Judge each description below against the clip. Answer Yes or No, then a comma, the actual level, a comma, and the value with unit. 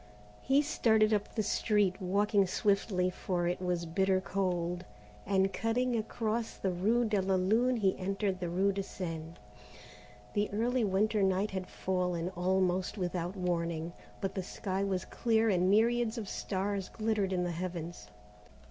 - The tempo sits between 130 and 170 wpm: Yes, average, 155 wpm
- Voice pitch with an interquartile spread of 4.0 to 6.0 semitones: No, average, 2.9 semitones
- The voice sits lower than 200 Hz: Yes, high, 190 Hz